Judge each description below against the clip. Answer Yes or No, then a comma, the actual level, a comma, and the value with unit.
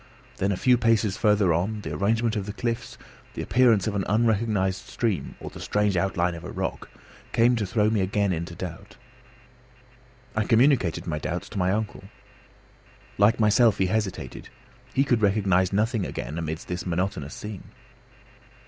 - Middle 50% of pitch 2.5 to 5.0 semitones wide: Yes, average, 3.3 semitones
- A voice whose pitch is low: Yes, low, 100 Hz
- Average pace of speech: Yes, average, 165 wpm